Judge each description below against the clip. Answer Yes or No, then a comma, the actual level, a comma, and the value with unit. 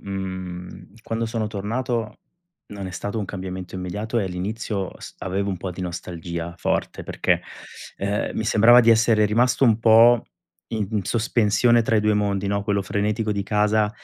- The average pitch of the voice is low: Yes, low, 105 Hz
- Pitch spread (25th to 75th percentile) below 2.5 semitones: No, average, 2.8 semitones